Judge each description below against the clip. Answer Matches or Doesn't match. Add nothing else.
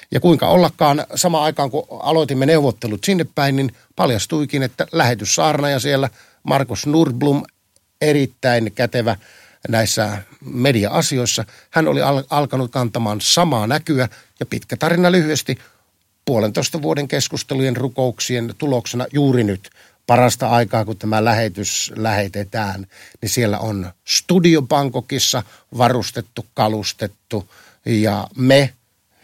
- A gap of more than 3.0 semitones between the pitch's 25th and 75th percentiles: Matches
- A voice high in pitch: Doesn't match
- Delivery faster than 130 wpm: Doesn't match